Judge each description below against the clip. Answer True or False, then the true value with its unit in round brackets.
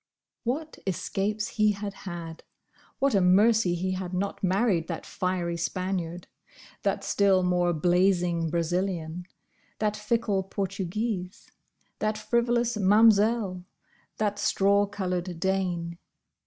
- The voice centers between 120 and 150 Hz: False (190 Hz)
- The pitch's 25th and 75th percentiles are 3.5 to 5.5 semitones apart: False (3.0 semitones)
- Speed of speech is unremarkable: False (110 wpm)